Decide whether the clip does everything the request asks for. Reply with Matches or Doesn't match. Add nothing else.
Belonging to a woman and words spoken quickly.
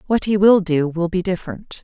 Matches